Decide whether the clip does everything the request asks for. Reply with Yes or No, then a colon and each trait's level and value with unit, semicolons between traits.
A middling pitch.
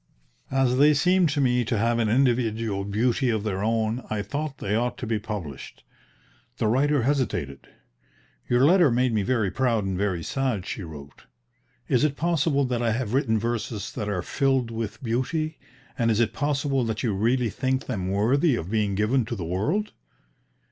No: low, 115 Hz